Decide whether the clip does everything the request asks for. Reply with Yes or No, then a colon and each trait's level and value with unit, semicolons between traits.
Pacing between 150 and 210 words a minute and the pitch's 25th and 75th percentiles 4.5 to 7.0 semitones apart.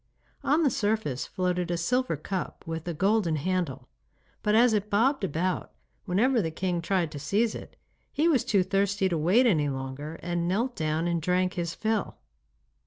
Yes: average, 175 wpm; average, 4.8 semitones